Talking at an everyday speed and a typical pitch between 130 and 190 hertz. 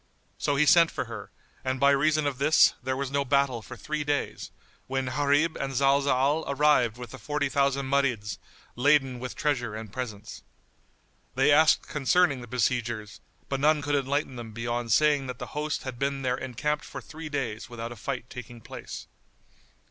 Yes: average, 180 wpm; low, 135 Hz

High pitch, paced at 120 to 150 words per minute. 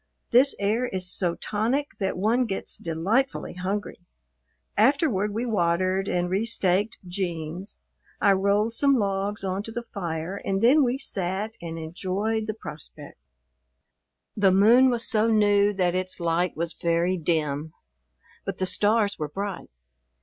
Yes: high, 195 Hz; average, 140 wpm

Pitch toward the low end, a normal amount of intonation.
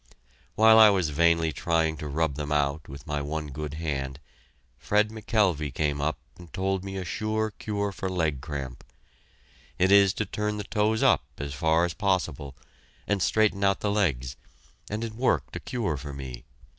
No: very low, 85 Hz; wide, 5.8 semitones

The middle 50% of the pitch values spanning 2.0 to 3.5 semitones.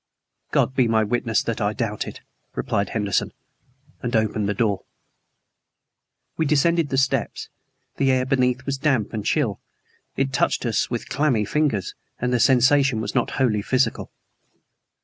No: average, 3.9 semitones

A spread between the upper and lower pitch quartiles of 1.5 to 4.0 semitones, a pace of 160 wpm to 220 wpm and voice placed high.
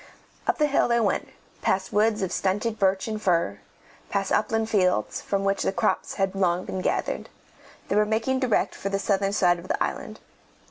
Yes: narrow, 2.5 semitones; average, 190 wpm; high, 200 Hz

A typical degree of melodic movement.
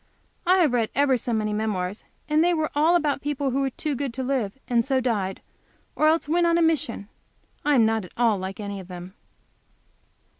No: wide, 5.9 semitones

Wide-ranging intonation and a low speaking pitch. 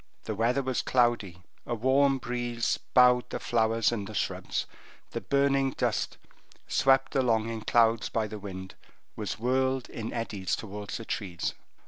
No: average, 3.0 semitones; low, 115 Hz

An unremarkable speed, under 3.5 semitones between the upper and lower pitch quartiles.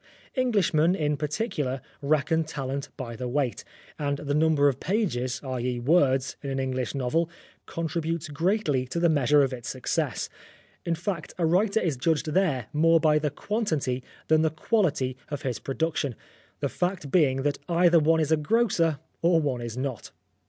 No: average, 165 wpm; average, 3.9 semitones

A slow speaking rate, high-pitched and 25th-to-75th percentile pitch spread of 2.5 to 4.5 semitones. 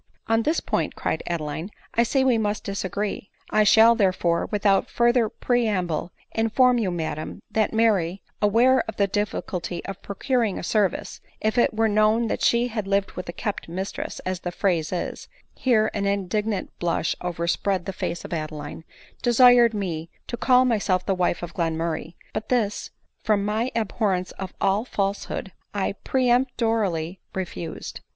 No: average, 165 wpm; high, 205 Hz; average, 3.9 semitones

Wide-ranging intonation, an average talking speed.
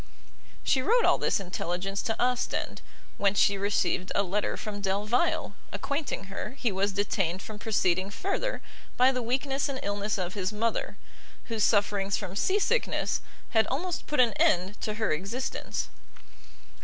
No: average, 4.4 semitones; average, 150 wpm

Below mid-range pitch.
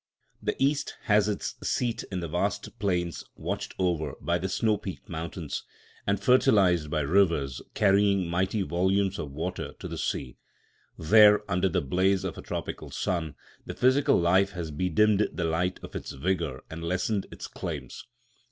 Yes: very low, 90 Hz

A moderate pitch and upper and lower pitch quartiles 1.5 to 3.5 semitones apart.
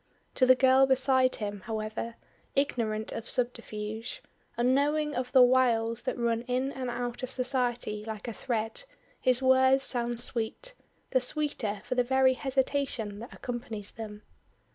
No: high, 245 Hz; narrow, 2.6 semitones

